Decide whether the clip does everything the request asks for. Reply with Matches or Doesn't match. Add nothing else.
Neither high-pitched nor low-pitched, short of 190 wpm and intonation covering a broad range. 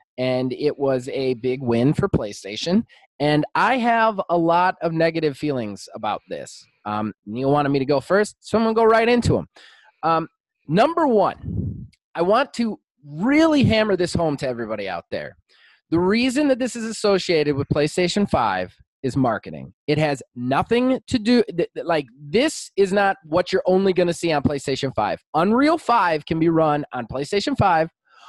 Matches